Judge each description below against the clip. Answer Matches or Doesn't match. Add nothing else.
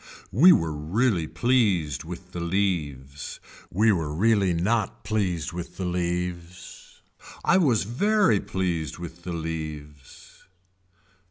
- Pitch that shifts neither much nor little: Matches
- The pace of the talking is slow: Matches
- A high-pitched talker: Doesn't match